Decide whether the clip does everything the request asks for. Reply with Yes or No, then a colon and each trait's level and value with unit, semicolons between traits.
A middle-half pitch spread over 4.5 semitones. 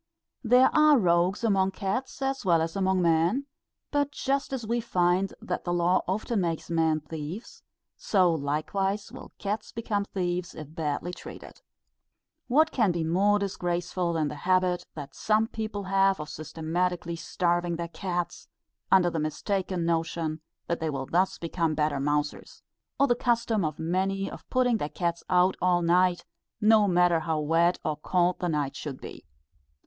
No: average, 3.5 semitones